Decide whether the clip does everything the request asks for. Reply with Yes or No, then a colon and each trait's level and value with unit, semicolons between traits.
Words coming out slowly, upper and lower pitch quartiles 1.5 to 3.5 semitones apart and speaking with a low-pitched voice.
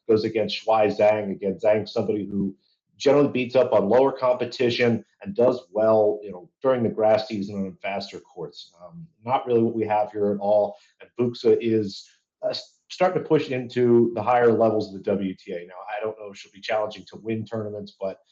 No: average, 200 wpm; average, 2.8 semitones; low, 110 Hz